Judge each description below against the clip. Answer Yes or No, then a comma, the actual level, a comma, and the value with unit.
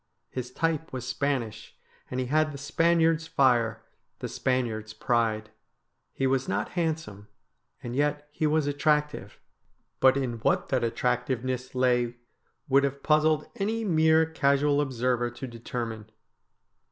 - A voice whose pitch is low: Yes, low, 130 Hz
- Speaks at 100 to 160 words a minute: Yes, average, 140 wpm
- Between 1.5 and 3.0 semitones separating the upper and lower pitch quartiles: No, average, 4.1 semitones